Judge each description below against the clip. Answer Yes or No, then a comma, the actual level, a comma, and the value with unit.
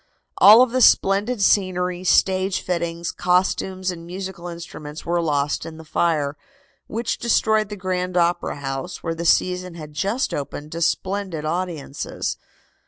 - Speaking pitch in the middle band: Yes, medium, 180 Hz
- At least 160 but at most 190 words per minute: No, average, 145 wpm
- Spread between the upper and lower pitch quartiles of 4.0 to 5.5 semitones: No, narrow, 2.6 semitones